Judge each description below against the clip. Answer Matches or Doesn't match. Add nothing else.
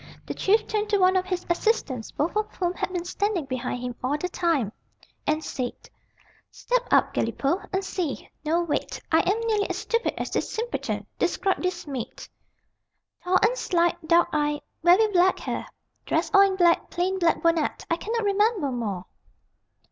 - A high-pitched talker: Matches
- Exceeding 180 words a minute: Doesn't match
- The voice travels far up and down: Doesn't match